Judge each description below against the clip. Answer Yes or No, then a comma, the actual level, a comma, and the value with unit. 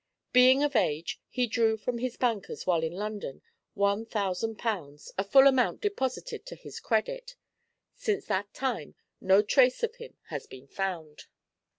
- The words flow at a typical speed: Yes, average, 160 wpm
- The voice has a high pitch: Yes, high, 225 Hz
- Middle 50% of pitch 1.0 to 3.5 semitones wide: No, wide, 5.6 semitones